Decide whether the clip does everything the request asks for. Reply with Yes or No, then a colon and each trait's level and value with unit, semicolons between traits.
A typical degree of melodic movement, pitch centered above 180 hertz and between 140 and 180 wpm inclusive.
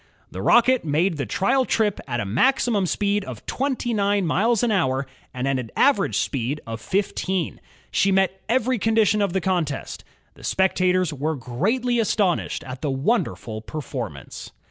No: wide, 7.8 semitones; high, 190 Hz; average, 165 wpm